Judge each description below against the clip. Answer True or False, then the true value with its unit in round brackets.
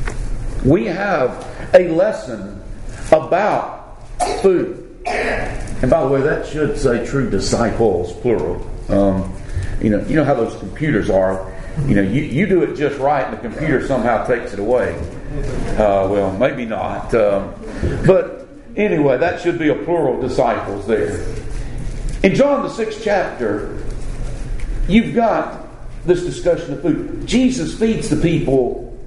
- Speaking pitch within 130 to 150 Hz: True (135 Hz)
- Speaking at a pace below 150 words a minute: True (140 wpm)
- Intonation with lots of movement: True (8.6 semitones)